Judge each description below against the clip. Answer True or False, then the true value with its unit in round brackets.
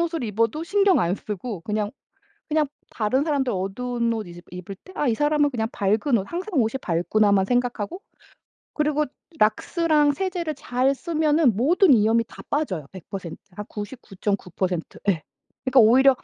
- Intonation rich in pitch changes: True (6.5 semitones)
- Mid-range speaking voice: False (245 Hz)